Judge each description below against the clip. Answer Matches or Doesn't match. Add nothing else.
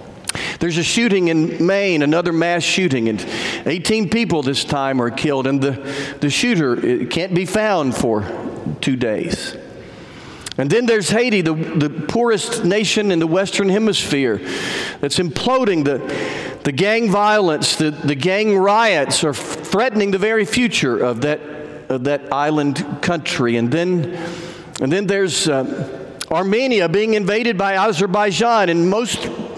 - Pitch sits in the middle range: Matches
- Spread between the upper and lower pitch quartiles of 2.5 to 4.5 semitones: Doesn't match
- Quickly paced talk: Doesn't match